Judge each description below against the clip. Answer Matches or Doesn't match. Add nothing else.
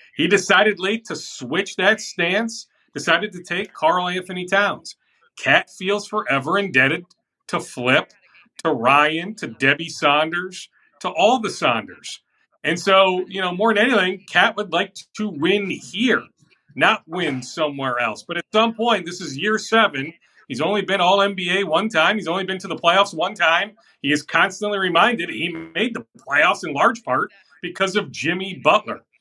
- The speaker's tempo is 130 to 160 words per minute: Doesn't match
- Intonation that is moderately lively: Matches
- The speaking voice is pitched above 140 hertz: Matches